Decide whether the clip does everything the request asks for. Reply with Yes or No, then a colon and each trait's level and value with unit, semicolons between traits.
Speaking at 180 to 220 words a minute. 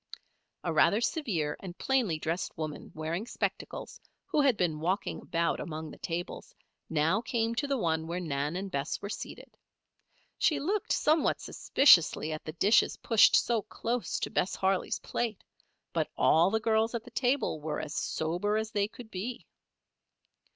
No: average, 165 wpm